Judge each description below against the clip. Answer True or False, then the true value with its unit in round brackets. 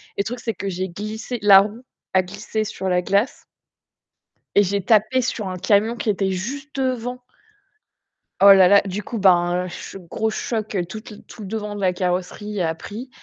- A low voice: False (205 Hz)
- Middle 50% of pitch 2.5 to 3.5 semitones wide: True (2.8 semitones)